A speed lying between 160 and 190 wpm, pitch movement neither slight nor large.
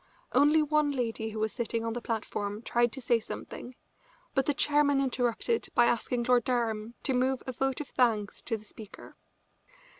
Yes: average, 180 wpm; average, 3.0 semitones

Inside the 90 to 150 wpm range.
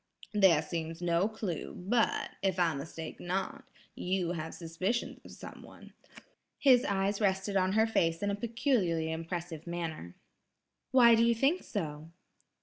Yes: average, 145 wpm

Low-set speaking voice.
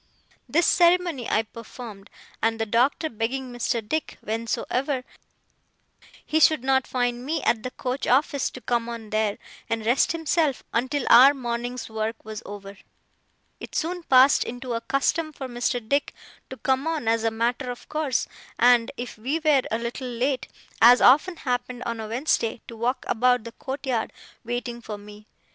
No: high, 245 Hz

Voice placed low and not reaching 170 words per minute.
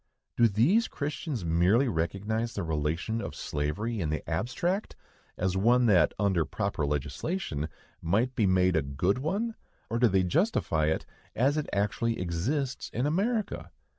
Yes: low, 105 Hz; average, 150 wpm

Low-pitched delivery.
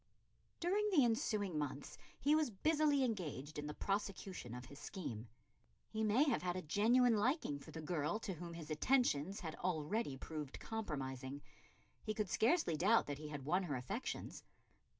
No: medium, 185 Hz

